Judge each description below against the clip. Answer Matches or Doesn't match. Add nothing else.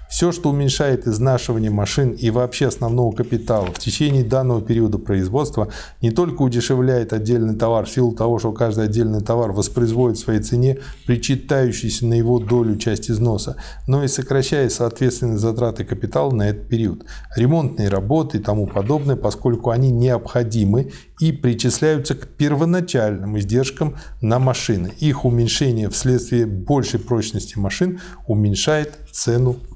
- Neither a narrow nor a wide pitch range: Matches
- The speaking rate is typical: Matches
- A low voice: Matches